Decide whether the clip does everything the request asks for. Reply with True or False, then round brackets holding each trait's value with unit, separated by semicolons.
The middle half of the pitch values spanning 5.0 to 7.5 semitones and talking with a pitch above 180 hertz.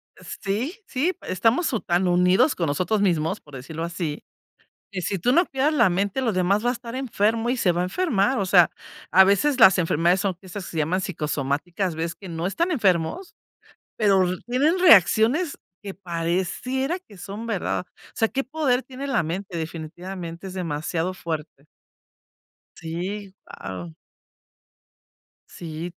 True (5.4 semitones; 190 Hz)